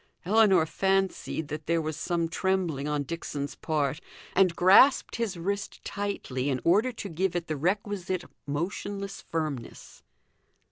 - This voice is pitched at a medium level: Yes, medium, 175 Hz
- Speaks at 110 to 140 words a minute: Yes, slow, 135 wpm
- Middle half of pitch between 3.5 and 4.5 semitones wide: Yes, average, 4.1 semitones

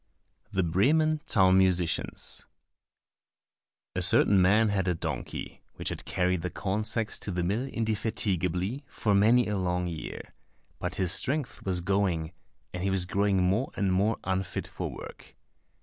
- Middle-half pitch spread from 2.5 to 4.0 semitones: Yes, average, 3.0 semitones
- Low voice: Yes, very low, 95 Hz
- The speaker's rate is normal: Yes, average, 155 wpm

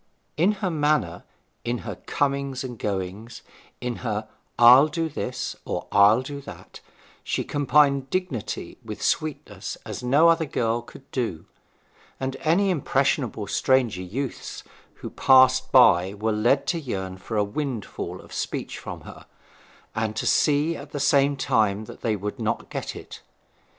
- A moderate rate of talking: Yes, average, 150 wpm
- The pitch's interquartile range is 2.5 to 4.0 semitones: No, average, 5.0 semitones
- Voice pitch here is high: No, low, 130 Hz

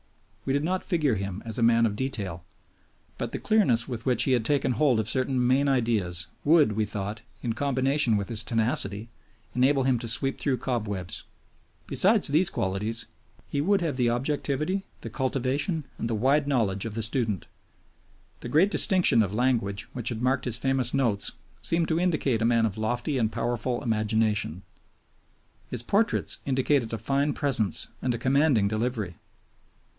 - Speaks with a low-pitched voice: Yes, low, 120 Hz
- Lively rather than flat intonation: No, average, 4.1 semitones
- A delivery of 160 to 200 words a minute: Yes, average, 170 wpm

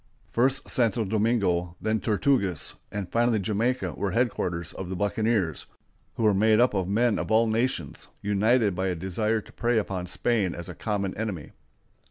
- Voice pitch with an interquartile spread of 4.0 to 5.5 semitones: No, average, 3.5 semitones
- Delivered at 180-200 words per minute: No, average, 170 wpm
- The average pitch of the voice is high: No, low, 105 Hz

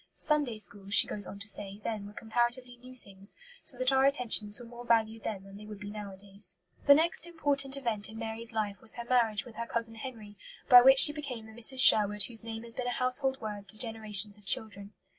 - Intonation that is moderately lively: Yes, average, 3.4 semitones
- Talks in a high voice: Yes, high, 225 Hz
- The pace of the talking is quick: Yes, fast, 225 wpm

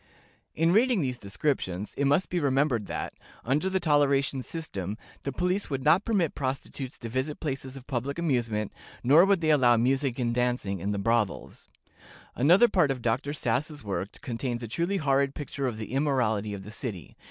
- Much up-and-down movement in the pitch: No, average, 4.4 semitones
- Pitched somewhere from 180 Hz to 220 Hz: No, low, 135 Hz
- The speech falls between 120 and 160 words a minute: No, average, 180 wpm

